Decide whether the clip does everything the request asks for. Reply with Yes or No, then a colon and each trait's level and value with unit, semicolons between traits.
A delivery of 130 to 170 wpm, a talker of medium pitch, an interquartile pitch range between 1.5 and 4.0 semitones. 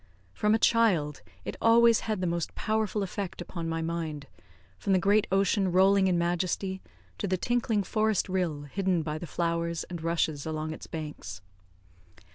Yes: average, 165 wpm; medium, 180 Hz; average, 3.6 semitones